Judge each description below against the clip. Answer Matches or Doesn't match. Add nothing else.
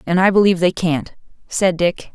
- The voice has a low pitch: Doesn't match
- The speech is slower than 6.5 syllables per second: Matches